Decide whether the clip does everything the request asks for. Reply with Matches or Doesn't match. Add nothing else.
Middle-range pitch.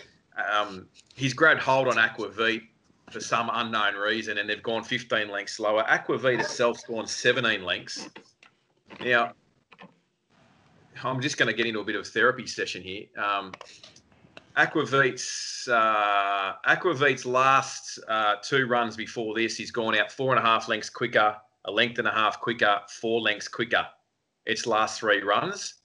Doesn't match